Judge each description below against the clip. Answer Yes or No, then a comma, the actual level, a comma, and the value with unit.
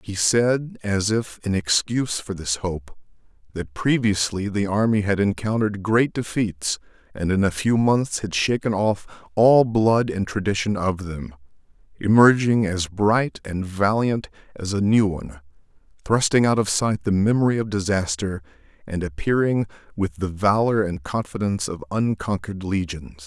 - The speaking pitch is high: No, low, 100 Hz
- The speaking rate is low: No, average, 150 wpm